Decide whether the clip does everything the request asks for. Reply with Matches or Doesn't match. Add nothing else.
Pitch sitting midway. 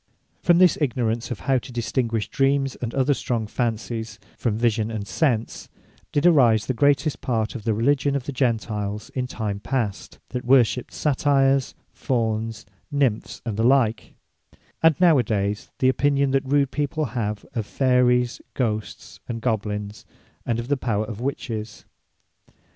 Doesn't match